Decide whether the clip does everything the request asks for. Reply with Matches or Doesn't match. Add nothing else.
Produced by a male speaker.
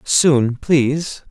Matches